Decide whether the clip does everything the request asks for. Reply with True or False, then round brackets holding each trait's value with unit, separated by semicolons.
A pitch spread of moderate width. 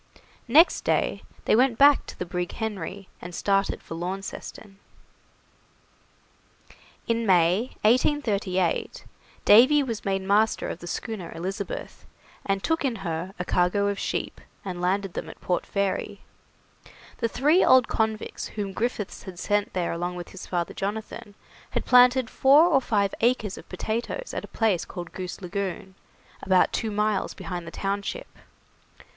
True (3.9 semitones)